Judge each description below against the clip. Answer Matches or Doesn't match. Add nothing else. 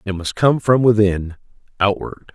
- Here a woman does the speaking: Doesn't match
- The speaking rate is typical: Matches